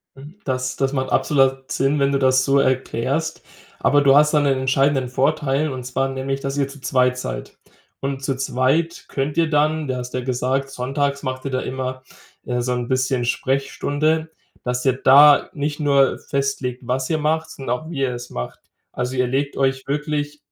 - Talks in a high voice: No, low, 135 Hz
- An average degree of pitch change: No, narrow, 1.9 semitones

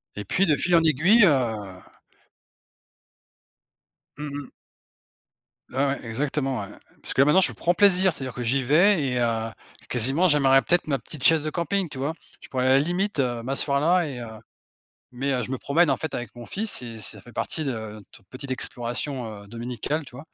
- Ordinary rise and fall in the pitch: Yes, average, 4.6 semitones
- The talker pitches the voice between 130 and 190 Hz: Yes, low, 135 Hz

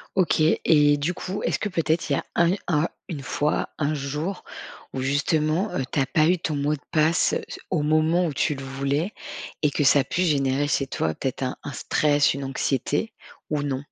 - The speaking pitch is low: No, medium, 150 Hz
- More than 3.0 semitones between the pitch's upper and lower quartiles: No, average, 2.7 semitones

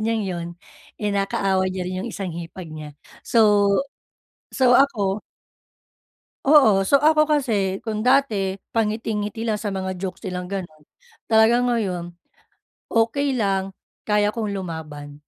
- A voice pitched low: No, high, 205 Hz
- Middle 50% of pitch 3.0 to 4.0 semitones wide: Yes, average, 3.4 semitones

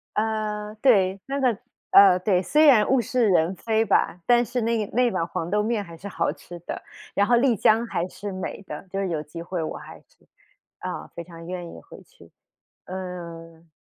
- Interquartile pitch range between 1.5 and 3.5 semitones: No, average, 4.3 semitones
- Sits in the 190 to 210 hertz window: Yes, high, 195 Hz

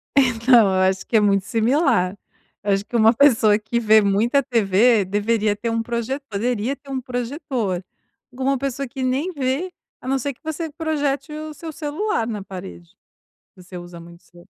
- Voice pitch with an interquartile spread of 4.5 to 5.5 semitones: Yes, average, 5.1 semitones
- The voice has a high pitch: Yes, high, 235 Hz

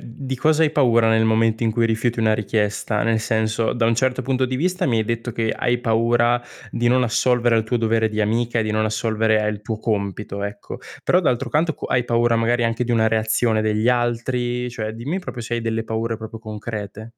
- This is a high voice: No, low, 115 Hz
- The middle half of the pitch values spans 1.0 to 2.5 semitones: Yes, narrow, 1.7 semitones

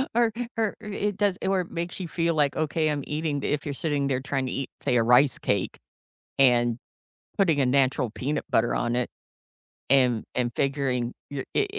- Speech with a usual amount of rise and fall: Yes, average, 4.7 semitones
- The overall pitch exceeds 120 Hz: Yes, medium, 140 Hz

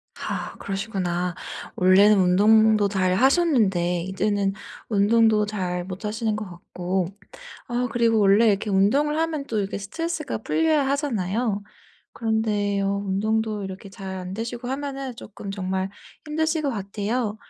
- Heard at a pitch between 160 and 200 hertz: No, high, 210 Hz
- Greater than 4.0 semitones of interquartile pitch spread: No, average, 3.5 semitones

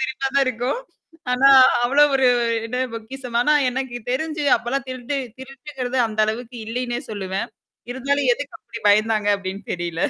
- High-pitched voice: Yes, very high, 250 Hz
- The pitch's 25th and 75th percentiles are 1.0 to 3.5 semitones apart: Yes, average, 3.2 semitones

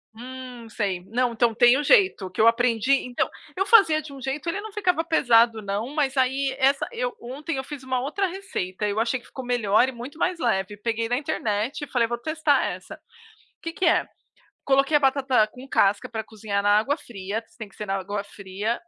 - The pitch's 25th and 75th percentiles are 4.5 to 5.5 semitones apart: Yes, average, 4.9 semitones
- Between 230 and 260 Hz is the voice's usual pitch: Yes, very high, 250 Hz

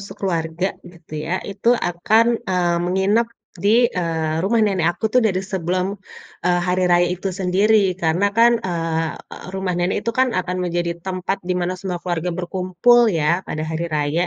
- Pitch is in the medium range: Yes, medium, 180 Hz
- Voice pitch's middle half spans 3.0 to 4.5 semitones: No, narrow, 2.5 semitones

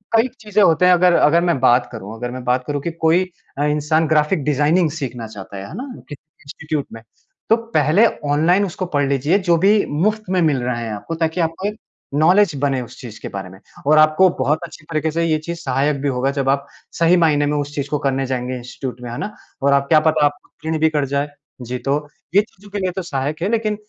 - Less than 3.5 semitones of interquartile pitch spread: No, average, 4.1 semitones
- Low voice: No, medium, 150 Hz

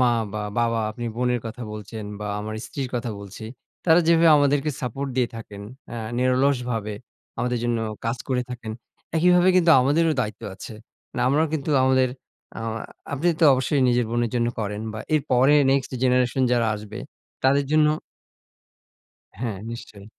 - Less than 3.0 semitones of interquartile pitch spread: No, average, 3.4 semitones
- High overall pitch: No, low, 125 Hz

